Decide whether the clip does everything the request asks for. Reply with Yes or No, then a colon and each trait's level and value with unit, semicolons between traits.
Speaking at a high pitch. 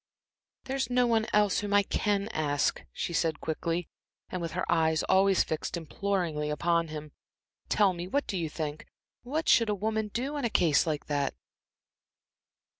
No: medium, 180 Hz